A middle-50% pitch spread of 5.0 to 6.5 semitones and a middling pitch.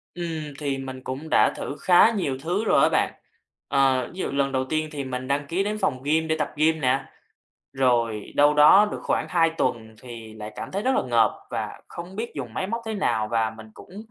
Yes: average, 5.3 semitones; medium, 145 Hz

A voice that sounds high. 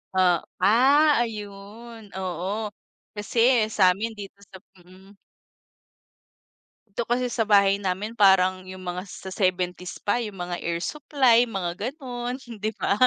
Yes: high, 200 Hz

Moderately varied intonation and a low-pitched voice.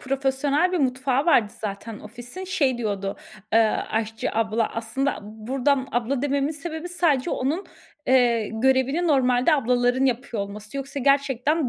No: average, 3.7 semitones; very high, 260 Hz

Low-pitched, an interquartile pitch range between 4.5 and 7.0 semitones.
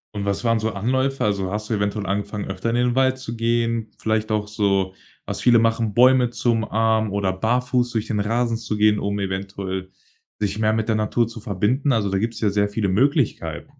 No: low, 110 Hz; narrow, 2.5 semitones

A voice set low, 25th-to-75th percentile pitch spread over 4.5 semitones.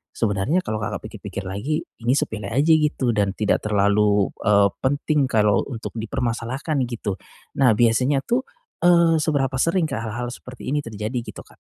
Yes: low, 120 Hz; wide, 5.4 semitones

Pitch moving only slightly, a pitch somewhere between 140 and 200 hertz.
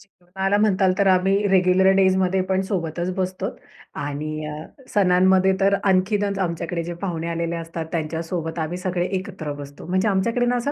Yes: narrow, 2.3 semitones; medium, 185 Hz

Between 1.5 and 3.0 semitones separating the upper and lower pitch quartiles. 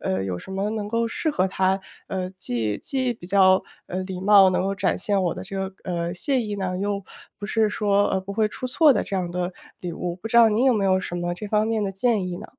Yes: average, 2.7 semitones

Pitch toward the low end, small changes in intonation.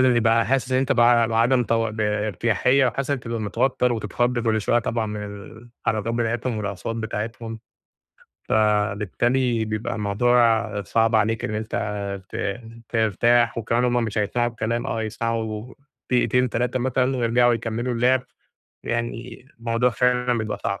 Yes: low, 115 Hz; narrow, 1.9 semitones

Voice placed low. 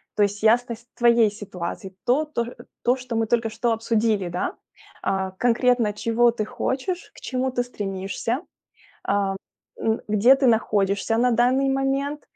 No: high, 230 Hz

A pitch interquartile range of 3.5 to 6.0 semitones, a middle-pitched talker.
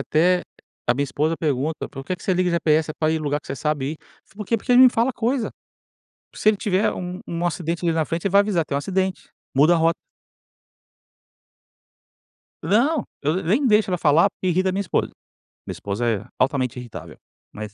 Yes: average, 4.5 semitones; medium, 170 Hz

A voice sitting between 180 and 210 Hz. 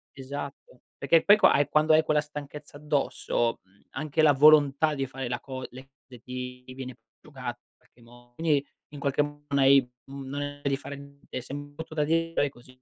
No: medium, 140 Hz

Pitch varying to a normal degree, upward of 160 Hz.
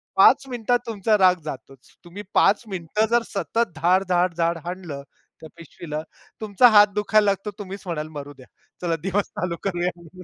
Yes: average, 3.7 semitones; medium, 185 Hz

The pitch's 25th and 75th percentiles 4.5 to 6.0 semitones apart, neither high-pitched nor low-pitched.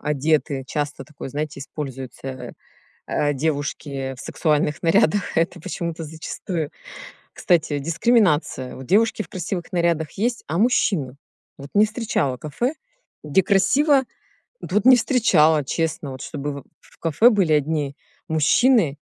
Yes: average, 5.1 semitones; medium, 155 Hz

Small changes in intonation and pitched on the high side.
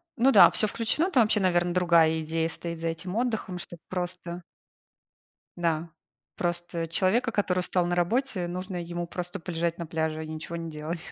No: narrow, 2.0 semitones; medium, 175 Hz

